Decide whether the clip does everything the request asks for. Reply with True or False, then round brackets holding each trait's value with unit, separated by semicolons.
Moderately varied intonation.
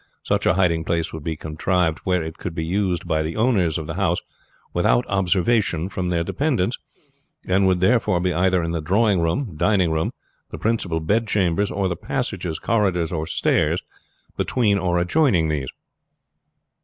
True (3.3 semitones)